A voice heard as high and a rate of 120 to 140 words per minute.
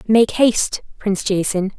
Yes: high, 205 Hz; slow, 135 wpm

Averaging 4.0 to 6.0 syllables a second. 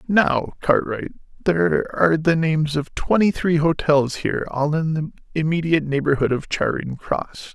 Yes: 4.7 syllables/s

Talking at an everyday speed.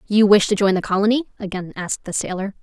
No: fast, 230 wpm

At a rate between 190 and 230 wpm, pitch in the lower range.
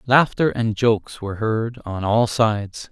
No: average, 165 wpm; low, 110 Hz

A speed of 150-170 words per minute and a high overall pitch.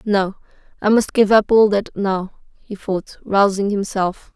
Yes: average, 165 wpm; high, 200 Hz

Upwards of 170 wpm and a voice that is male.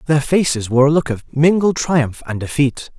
Yes: average, 200 wpm; male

